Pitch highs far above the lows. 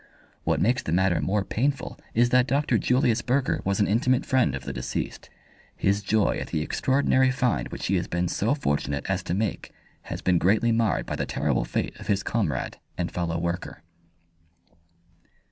Yes: wide, 6.1 semitones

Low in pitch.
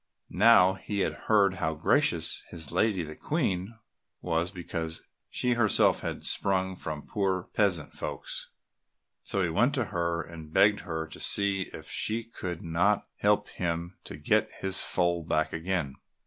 Yes: very low, 90 Hz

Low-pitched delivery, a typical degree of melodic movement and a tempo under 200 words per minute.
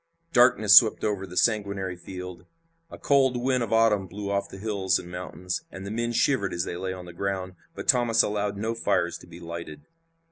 No: low, 100 Hz; average, 3.6 semitones; fast, 205 wpm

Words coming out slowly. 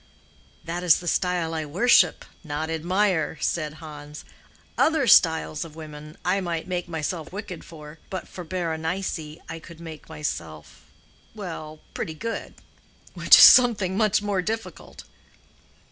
Yes: slow, 130 wpm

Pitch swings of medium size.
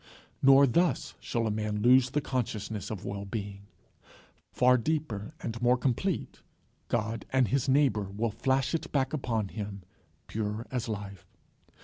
Yes: average, 4.0 semitones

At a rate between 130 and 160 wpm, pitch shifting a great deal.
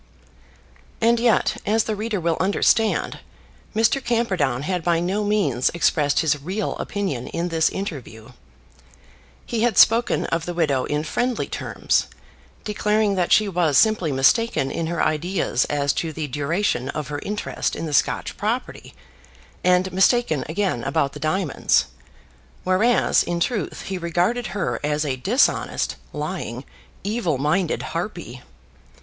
Yes: average, 140 wpm; wide, 6.0 semitones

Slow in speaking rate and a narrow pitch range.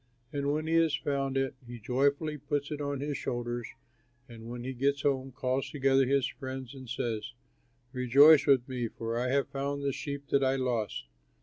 No: average, 190 wpm; narrow, 2.3 semitones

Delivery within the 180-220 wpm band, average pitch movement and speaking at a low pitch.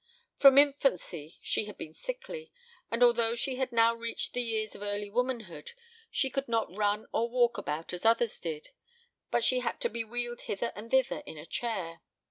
No: average, 190 wpm; average, 3.4 semitones; high, 230 Hz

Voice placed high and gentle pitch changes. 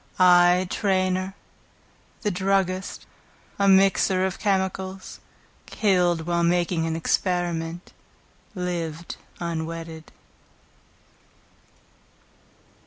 No: medium, 180 Hz; narrow, 1.9 semitones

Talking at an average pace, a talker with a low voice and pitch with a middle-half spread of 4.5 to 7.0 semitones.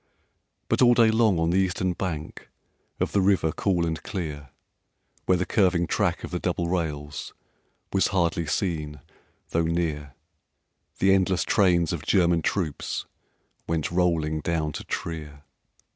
No: average, 145 wpm; very low, 85 Hz; average, 3.0 semitones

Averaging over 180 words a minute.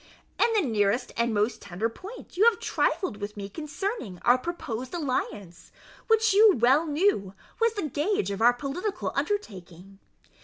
No: average, 155 wpm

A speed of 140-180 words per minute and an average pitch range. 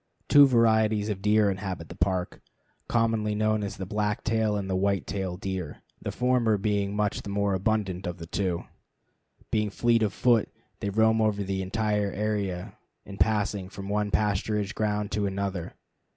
No: average, 165 wpm; narrow, 1.9 semitones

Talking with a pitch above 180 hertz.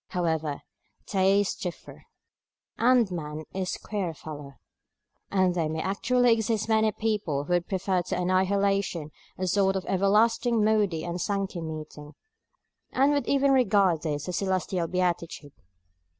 Yes: high, 190 Hz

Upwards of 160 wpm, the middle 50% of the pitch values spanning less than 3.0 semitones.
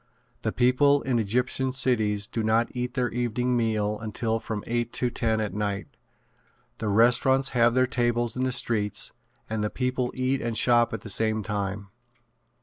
Yes: average, 170 wpm; narrow, 2.5 semitones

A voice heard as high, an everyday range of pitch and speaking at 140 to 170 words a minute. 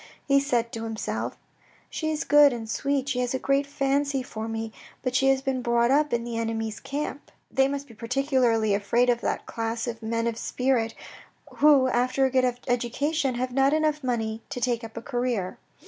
No: very high, 250 Hz; average, 3.1 semitones; average, 200 wpm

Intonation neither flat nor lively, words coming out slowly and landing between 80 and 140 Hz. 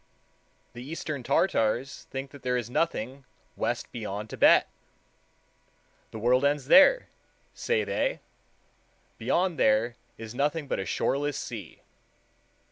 Yes: average, 4.3 semitones; slow, 120 wpm; low, 135 Hz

